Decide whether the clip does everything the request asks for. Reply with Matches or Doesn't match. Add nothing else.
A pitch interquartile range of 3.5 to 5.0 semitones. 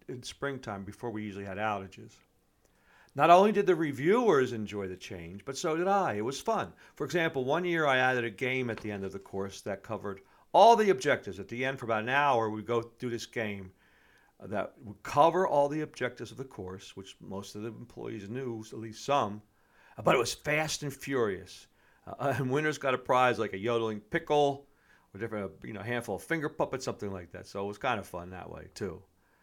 Doesn't match